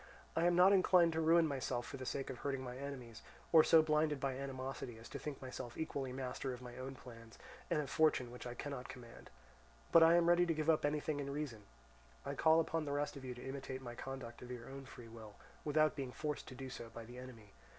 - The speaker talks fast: Yes, fast, 240 wpm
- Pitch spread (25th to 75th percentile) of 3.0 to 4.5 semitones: Yes, average, 3.6 semitones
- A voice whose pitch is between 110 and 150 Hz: Yes, low, 135 Hz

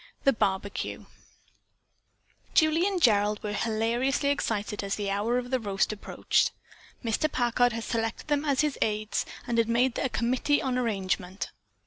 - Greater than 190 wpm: No, average, 150 wpm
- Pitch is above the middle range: Yes, high, 230 Hz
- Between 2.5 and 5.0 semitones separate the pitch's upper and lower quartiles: Yes, average, 4.0 semitones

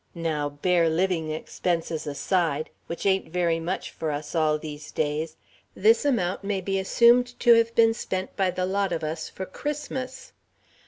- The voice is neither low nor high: Yes, medium, 180 Hz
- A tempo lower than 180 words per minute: Yes, average, 165 wpm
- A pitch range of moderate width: Yes, average, 4.1 semitones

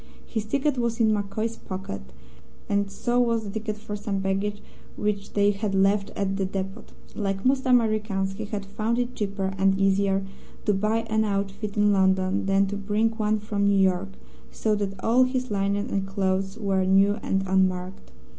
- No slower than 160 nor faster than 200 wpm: Yes, average, 180 wpm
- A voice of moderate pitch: No, high, 200 Hz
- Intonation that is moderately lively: No, narrow, 1.9 semitones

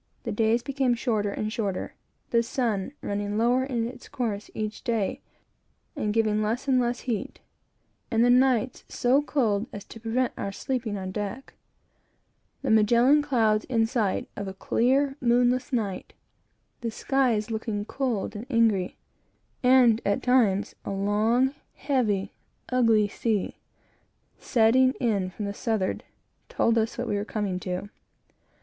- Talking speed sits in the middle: Yes, average, 145 wpm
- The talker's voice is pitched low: No, high, 225 Hz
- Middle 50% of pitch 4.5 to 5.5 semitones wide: No, average, 3.3 semitones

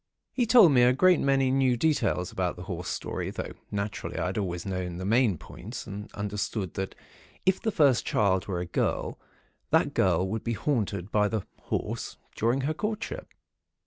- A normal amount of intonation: No, wide, 6.2 semitones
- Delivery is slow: No, average, 180 wpm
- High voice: No, low, 105 Hz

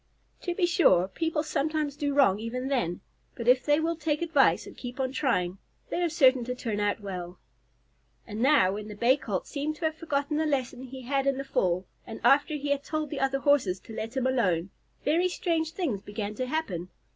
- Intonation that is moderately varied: No, wide, 5.9 semitones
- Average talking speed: No, fast, 215 wpm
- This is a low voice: No, very high, 270 Hz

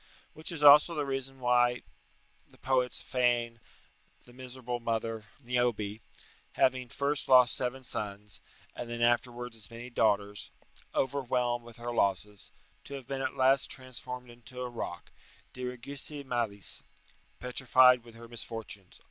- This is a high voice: No, low, 125 Hz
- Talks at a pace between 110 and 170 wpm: Yes, slow, 135 wpm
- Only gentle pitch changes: Yes, narrow, 1.9 semitones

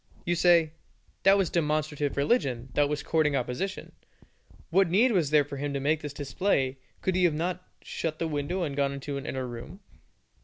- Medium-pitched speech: Yes, medium, 150 Hz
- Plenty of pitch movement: No, average, 3.9 semitones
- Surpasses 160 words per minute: Yes, average, 190 wpm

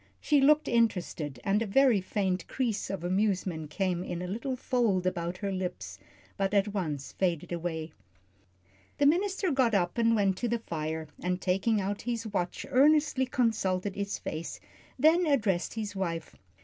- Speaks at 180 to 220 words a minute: No, average, 160 wpm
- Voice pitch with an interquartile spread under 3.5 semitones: No, average, 4.8 semitones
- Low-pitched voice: No, high, 195 Hz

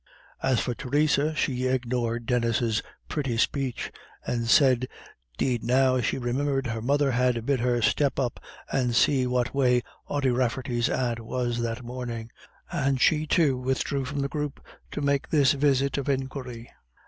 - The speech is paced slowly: No, average, 155 wpm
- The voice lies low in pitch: Yes, low, 130 Hz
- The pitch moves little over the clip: Yes, narrow, 2.3 semitones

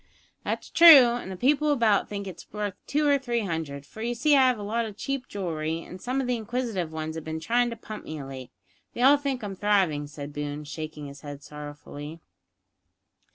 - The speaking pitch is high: Yes, high, 200 Hz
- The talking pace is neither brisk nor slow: No, fast, 215 wpm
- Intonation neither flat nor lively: No, wide, 8.0 semitones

